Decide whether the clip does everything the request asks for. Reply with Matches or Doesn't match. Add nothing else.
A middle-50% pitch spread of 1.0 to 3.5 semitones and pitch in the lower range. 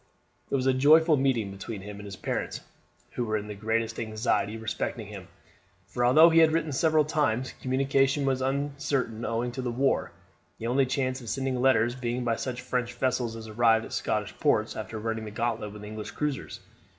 Matches